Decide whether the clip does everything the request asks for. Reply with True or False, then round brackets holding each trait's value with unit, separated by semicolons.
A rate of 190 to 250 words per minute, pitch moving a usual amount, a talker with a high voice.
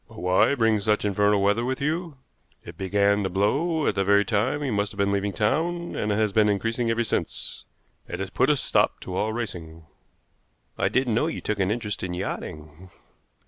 False (200 wpm; 3.6 semitones; 105 Hz)